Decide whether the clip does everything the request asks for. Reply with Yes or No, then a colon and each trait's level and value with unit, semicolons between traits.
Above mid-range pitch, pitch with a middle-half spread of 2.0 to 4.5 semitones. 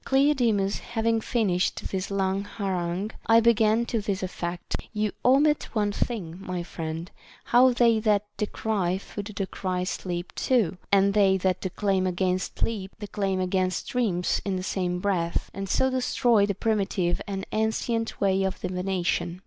Yes: high, 195 Hz; average, 3.2 semitones